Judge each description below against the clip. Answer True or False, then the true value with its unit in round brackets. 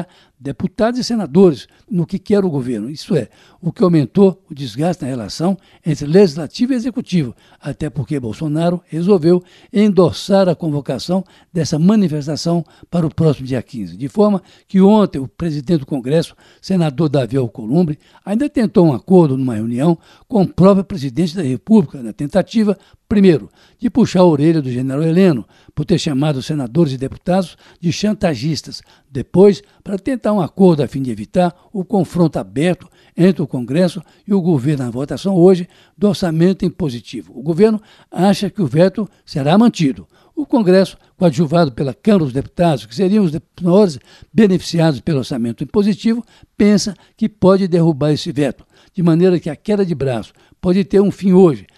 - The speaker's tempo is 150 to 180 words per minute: True (165 wpm)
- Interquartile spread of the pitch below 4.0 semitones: False (4.6 semitones)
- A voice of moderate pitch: True (175 Hz)